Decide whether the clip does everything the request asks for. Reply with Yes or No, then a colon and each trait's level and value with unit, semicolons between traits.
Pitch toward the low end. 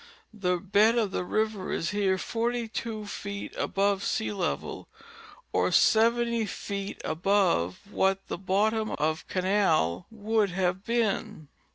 No: high, 200 Hz